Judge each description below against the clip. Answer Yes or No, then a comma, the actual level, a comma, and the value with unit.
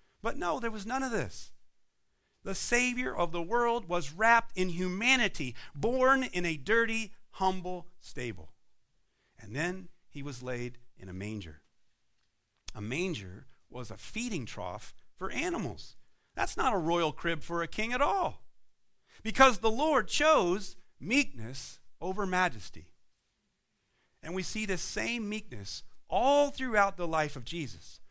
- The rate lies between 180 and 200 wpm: No, average, 145 wpm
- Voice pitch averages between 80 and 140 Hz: No, medium, 180 Hz